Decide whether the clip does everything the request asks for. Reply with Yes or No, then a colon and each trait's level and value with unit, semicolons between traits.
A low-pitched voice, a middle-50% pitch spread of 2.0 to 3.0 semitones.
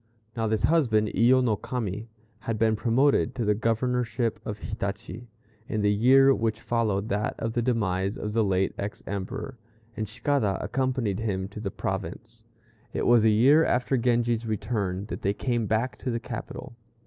Yes: low, 115 Hz; average, 2.7 semitones